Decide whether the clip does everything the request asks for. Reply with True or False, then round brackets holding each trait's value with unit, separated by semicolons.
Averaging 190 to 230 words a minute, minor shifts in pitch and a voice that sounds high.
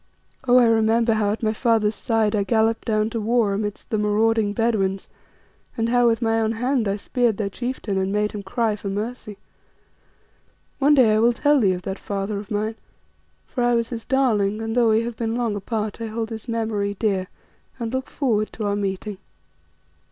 True (200 wpm; 2.1 semitones; 220 Hz)